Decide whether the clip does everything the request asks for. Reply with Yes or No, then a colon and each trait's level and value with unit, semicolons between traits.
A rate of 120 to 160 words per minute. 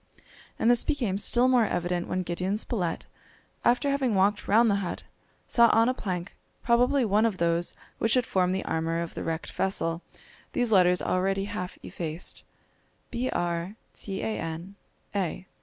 Yes: average, 155 wpm